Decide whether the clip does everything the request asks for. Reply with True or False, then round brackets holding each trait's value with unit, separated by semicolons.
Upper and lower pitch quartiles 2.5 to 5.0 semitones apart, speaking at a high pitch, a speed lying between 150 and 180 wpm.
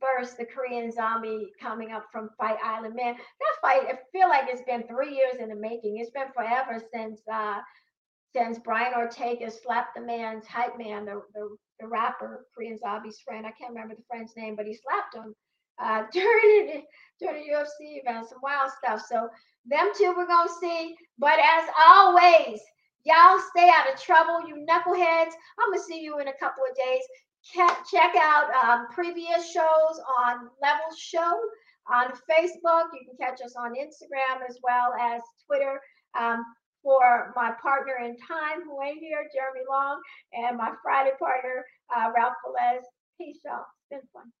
False (5.6 semitones; 260 Hz; 175 wpm)